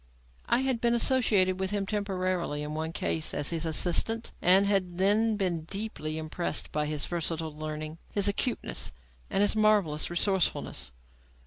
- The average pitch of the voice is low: No, medium, 185 Hz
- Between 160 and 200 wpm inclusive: No, average, 150 wpm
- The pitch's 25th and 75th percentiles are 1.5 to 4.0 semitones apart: No, average, 4.6 semitones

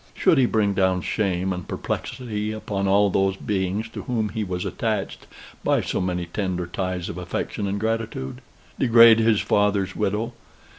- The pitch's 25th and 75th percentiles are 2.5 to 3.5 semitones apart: Yes, average, 2.9 semitones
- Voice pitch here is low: Yes, low, 100 Hz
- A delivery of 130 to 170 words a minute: Yes, average, 160 wpm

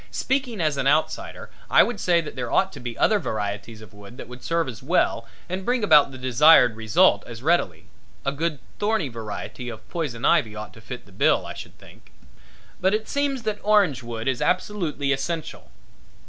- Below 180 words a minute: No, average, 195 wpm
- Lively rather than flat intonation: Yes, wide, 7.9 semitones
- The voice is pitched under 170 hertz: Yes, medium, 140 Hz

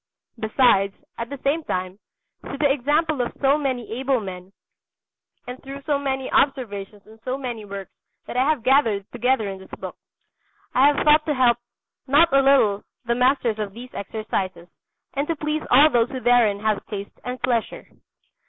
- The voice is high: Yes, very high, 250 Hz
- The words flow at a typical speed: Yes, average, 175 wpm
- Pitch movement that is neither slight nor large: Yes, average, 4.5 semitones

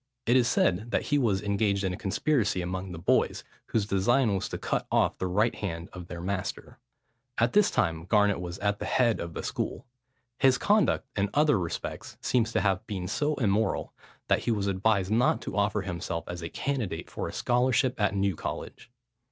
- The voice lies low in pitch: Yes, low, 100 Hz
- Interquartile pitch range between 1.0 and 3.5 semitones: No, average, 4.3 semitones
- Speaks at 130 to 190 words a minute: No, average, 200 wpm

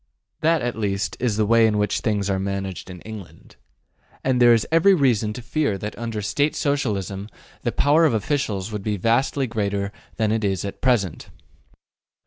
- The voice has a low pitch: Yes, low, 110 Hz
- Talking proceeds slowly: No, average, 180 wpm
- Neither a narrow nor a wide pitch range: Yes, average, 3.9 semitones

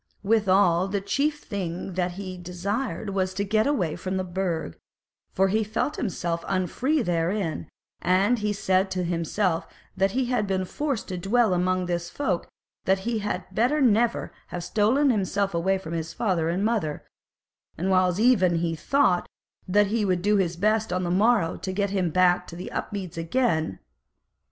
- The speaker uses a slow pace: No, average, 175 wpm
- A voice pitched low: No, high, 190 Hz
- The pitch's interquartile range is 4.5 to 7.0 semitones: No, average, 3.2 semitones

